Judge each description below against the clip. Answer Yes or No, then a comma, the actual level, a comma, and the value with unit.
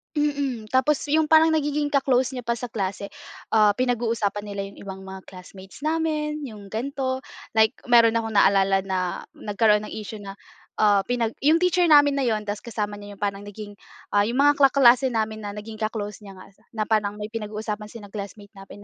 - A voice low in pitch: No, high, 220 Hz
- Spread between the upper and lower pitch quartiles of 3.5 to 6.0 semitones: Yes, average, 4.4 semitones